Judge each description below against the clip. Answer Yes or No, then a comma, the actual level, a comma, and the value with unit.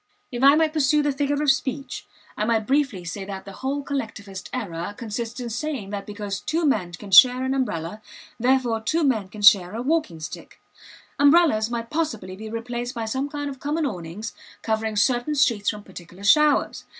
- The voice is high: Yes, high, 235 Hz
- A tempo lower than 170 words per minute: No, average, 185 wpm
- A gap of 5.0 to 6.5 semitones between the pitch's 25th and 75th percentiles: Yes, wide, 5.5 semitones